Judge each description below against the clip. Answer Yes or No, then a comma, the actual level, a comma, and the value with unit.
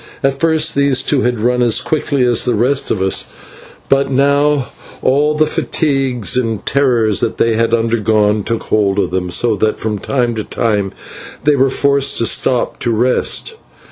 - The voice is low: Yes, low, 125 Hz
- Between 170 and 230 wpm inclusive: Yes, average, 175 wpm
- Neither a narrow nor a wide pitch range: Yes, average, 4.0 semitones